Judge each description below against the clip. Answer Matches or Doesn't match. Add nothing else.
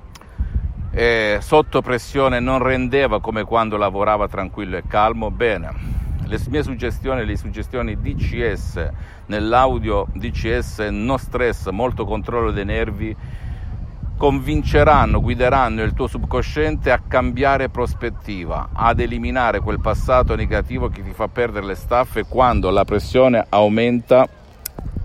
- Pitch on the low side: Matches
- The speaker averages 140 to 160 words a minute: Doesn't match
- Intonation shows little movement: Doesn't match